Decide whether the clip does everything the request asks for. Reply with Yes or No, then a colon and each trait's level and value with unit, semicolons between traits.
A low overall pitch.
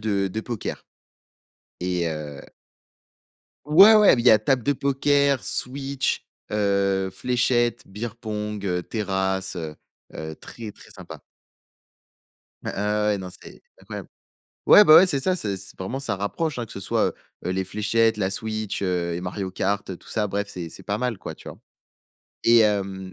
Yes: low, 105 Hz